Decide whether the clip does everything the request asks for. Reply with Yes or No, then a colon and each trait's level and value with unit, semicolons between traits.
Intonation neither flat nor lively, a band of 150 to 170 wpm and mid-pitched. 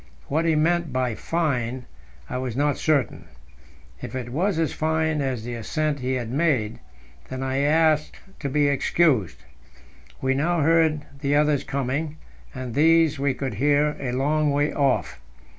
Yes: average, 3.2 semitones; average, 160 wpm; medium, 145 Hz